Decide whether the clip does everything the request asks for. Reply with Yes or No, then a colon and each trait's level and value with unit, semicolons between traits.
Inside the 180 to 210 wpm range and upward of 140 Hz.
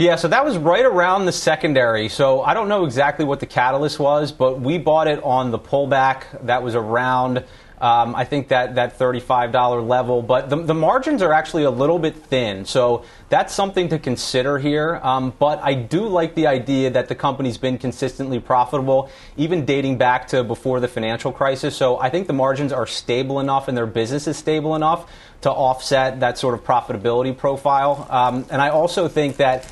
No: average, 200 wpm; low, 135 Hz